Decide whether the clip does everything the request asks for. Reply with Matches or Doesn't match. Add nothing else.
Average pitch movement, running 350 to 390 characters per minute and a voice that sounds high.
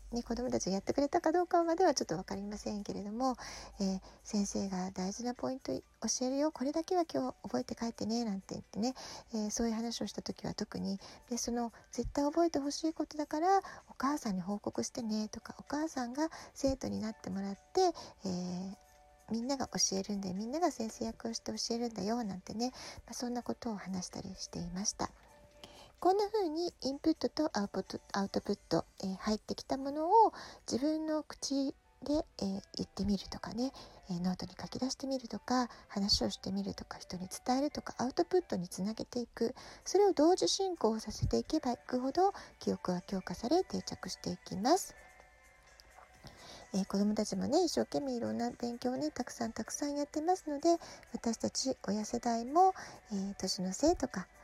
Doesn't match